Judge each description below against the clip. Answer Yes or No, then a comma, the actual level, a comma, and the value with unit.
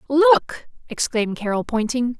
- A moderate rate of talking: No, slow, 110 wpm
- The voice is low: No, very high, 255 Hz